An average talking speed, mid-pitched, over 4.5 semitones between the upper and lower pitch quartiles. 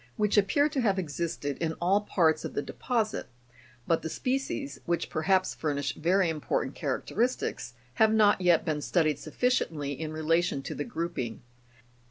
Yes: average, 170 wpm; medium, 170 Hz; average, 5.2 semitones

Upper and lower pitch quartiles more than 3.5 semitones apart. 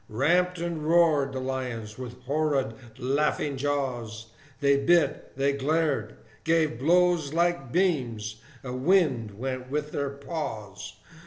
Yes: average, 4.1 semitones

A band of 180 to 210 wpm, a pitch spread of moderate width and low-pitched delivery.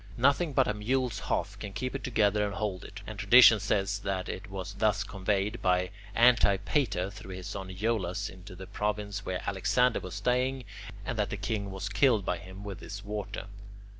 Yes: average, 190 wpm; average, 3.0 semitones; low, 100 Hz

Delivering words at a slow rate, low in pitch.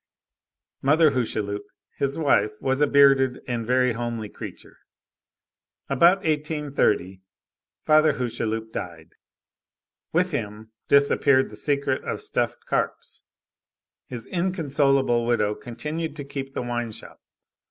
Yes: slow, 115 wpm; low, 130 Hz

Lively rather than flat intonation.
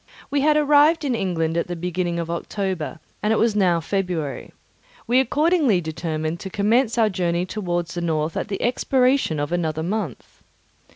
Yes: wide, 5.7 semitones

